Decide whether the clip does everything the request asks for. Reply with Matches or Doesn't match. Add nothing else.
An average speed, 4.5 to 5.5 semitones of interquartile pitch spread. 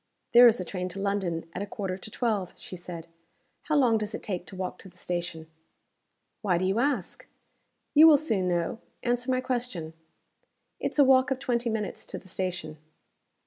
Matches